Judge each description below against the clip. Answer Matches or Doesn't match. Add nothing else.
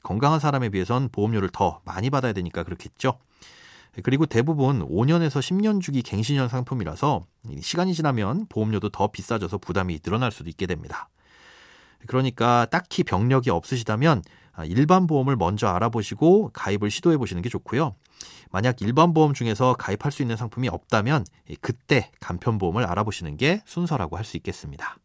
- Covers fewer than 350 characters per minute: Doesn't match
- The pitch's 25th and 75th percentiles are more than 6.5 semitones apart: Doesn't match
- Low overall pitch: Matches